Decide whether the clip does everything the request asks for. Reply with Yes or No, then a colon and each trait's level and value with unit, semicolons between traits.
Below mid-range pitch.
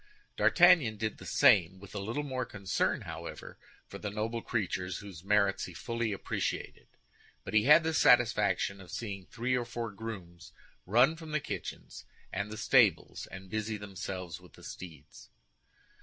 Yes: low, 105 Hz